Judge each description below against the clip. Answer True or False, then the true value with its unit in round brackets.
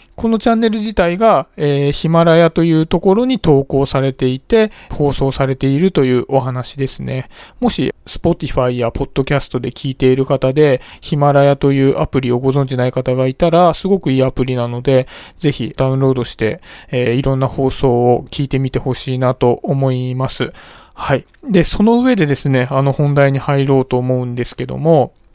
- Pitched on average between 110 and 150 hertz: True (135 Hz)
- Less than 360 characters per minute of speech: False (375 characters per minute)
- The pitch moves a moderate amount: True (3.5 semitones)